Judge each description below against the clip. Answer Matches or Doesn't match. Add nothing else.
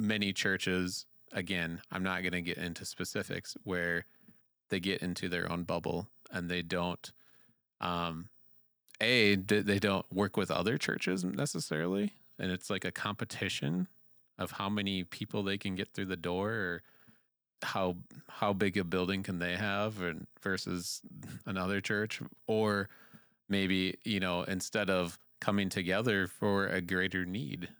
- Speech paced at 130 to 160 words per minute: Matches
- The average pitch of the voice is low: Matches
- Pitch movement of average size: Doesn't match